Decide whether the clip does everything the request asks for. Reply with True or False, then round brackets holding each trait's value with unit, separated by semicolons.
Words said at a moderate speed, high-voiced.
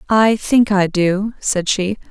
True (170 wpm; 200 Hz)